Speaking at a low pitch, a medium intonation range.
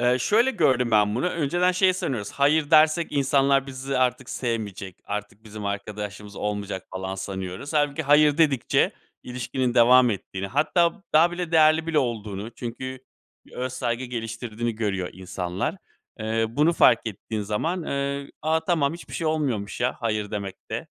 No: low, 125 Hz; wide, 6.2 semitones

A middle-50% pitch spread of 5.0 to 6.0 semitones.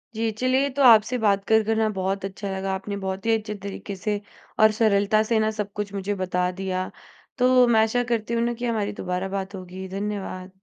No: narrow, 2.5 semitones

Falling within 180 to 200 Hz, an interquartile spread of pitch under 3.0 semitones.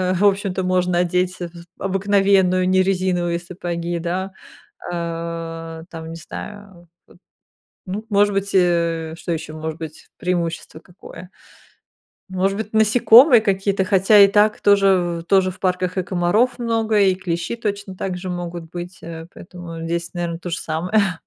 Yes: medium, 185 Hz; narrow, 2.5 semitones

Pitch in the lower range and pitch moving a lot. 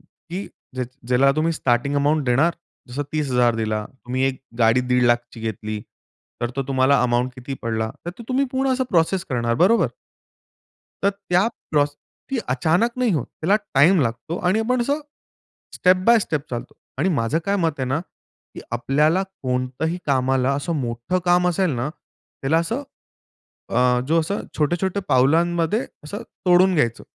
No: medium, 145 Hz; wide, 6.2 semitones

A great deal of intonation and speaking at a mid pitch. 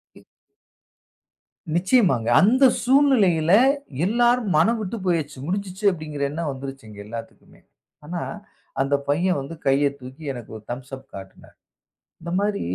Yes: wide, 6.9 semitones; medium, 165 Hz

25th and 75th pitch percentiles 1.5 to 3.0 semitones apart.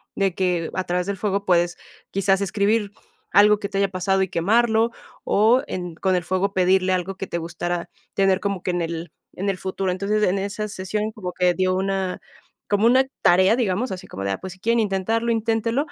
Yes: narrow, 2.4 semitones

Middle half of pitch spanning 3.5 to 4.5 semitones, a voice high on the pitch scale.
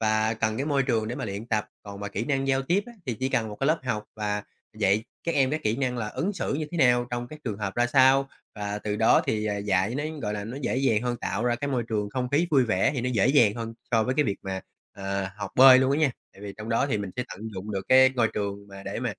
No: average, 4.1 semitones; low, 115 Hz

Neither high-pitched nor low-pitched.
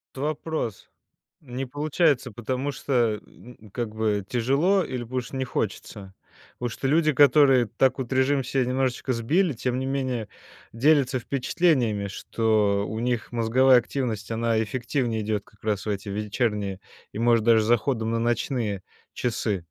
No: low, 120 Hz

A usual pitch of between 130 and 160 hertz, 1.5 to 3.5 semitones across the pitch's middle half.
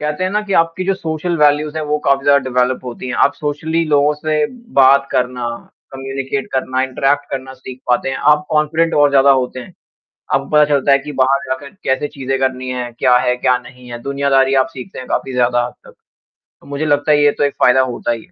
Yes: medium, 140 Hz; narrow, 2.5 semitones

